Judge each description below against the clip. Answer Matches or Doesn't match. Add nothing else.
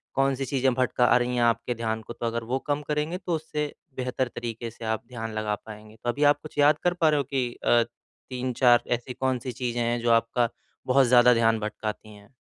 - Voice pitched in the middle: Doesn't match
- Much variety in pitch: Doesn't match